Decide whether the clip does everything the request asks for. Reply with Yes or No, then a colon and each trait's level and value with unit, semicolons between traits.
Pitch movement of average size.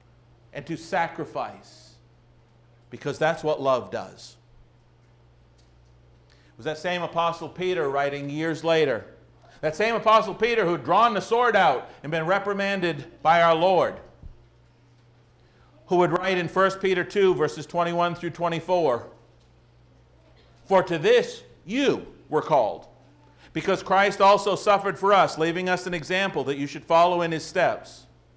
No: wide, 7.5 semitones